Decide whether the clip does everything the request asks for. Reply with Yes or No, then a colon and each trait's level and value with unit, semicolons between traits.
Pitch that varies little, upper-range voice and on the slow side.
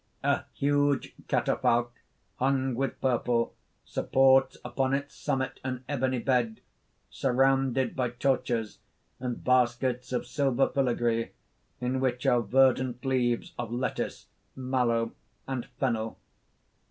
No: narrow, 1.7 semitones; low, 130 Hz; slow, 115 wpm